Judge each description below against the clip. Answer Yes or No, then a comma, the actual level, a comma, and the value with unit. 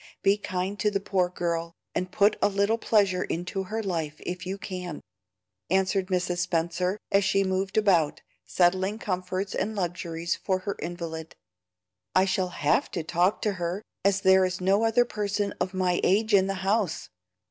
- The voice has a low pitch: No, medium, 185 Hz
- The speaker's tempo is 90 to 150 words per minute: No, average, 170 wpm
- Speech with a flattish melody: Yes, narrow, 2.1 semitones